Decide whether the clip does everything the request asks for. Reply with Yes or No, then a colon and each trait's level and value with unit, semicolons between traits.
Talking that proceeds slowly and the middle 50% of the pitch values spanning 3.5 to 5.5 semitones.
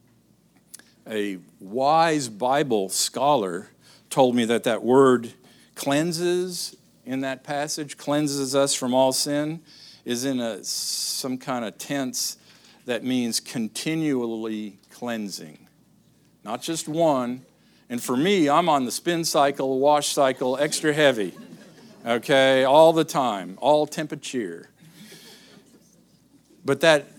Yes: slow, 115 wpm; average, 3.8 semitones